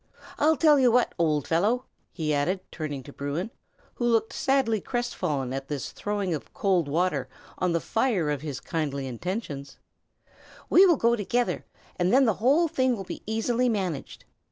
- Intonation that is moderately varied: No, wide, 8.3 semitones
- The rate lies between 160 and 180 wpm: Yes, average, 170 wpm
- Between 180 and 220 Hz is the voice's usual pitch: Yes, high, 190 Hz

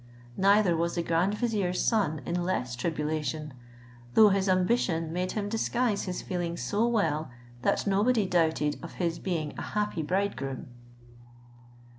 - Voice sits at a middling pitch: Yes, medium, 180 Hz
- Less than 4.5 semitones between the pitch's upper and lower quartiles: Yes, average, 4.0 semitones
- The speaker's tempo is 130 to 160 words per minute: Yes, average, 140 wpm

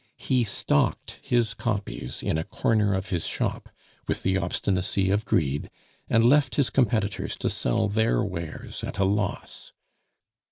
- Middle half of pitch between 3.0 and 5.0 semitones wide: Yes, average, 3.3 semitones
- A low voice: Yes, low, 100 Hz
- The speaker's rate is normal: Yes, average, 150 wpm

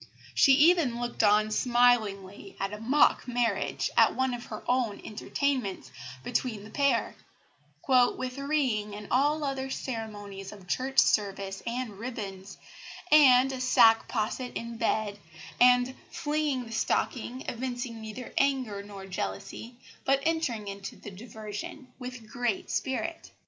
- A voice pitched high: Yes, high, 240 Hz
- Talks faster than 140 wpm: No, slow, 135 wpm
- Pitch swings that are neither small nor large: Yes, average, 3.8 semitones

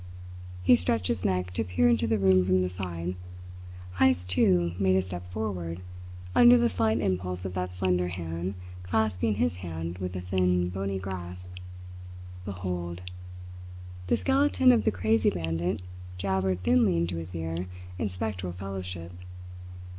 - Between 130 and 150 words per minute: Yes, average, 145 wpm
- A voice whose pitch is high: No, very low, 90 Hz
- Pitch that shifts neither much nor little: No, narrow, 1.6 semitones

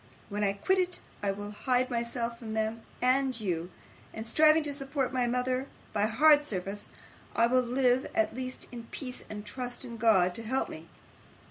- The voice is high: Yes, high, 240 Hz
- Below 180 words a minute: No, average, 185 wpm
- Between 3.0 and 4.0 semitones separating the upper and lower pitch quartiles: Yes, average, 3.3 semitones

